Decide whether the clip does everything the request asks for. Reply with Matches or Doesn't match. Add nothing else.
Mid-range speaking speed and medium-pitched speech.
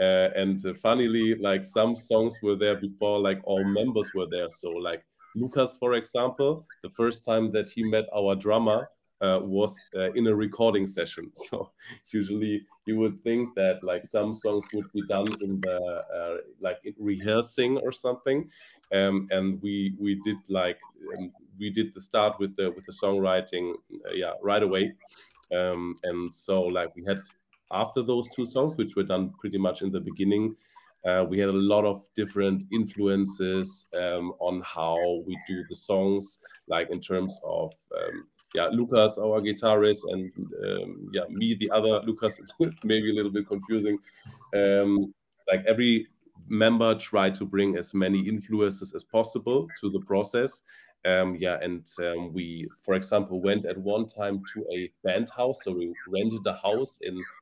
Doesn't match